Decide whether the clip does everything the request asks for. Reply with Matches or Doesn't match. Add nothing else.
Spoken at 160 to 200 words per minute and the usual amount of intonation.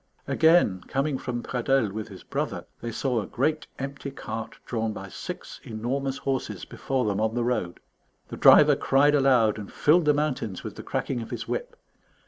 Matches